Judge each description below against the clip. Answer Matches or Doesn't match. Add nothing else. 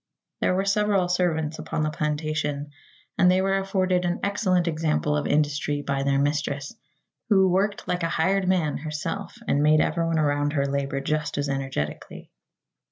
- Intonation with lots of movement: Doesn't match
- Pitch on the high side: Doesn't match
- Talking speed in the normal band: Matches